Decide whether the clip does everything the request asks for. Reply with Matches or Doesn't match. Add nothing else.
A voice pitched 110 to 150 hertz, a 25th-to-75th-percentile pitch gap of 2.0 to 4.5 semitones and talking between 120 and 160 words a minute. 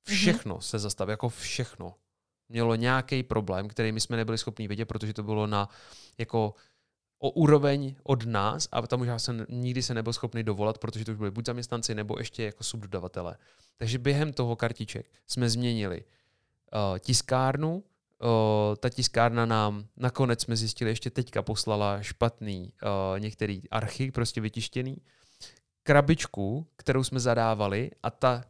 Matches